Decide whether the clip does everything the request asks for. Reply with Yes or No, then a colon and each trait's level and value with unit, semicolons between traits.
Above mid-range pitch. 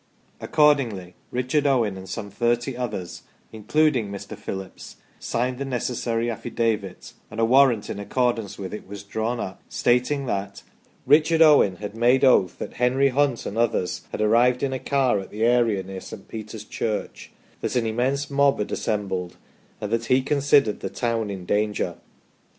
No: low, 115 Hz